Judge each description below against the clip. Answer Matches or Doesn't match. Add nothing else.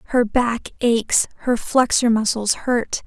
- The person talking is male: Doesn't match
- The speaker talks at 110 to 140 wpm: Matches